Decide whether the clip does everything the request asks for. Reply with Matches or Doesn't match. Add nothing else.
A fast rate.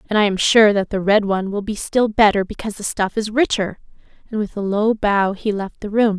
Matches